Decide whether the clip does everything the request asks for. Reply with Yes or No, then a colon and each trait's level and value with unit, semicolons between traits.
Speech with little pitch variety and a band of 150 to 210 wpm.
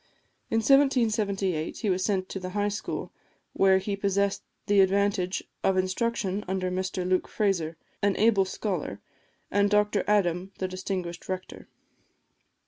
No: narrow, 1.8 semitones; slow, 135 wpm